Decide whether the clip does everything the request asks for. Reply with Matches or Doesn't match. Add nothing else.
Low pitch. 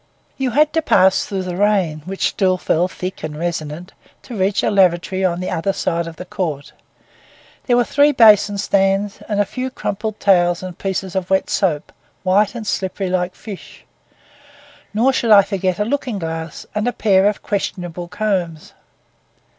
Doesn't match